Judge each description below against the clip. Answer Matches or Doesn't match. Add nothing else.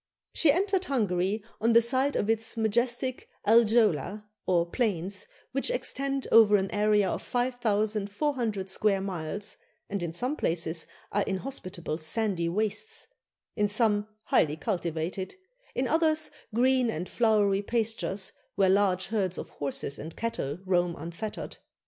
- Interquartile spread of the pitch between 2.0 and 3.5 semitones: Doesn't match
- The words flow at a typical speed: Doesn't match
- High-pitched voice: Matches